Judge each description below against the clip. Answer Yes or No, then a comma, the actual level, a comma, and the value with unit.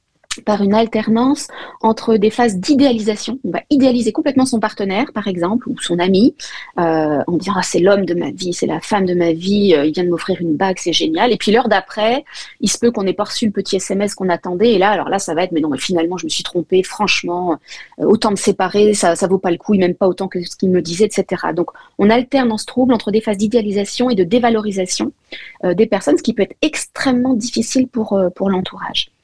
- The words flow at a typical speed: No, fast, 245 wpm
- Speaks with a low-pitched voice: No, high, 205 Hz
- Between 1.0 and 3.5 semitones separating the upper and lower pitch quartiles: No, average, 4.1 semitones